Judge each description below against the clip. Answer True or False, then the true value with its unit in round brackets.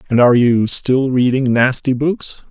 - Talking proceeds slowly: False (170 wpm)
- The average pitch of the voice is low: True (130 Hz)